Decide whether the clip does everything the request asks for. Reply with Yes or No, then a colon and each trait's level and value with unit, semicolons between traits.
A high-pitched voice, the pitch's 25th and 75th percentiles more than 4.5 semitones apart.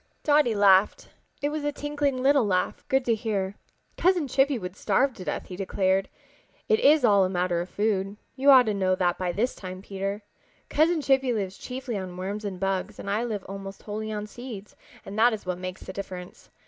Yes: high, 205 Hz; wide, 5.4 semitones